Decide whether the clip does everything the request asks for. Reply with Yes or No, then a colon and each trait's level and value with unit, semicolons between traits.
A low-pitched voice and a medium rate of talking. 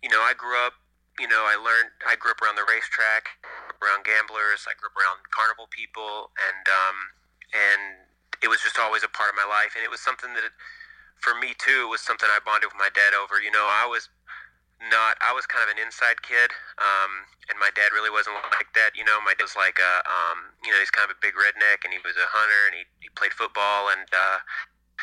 No: low, 105 Hz; fast, 240 wpm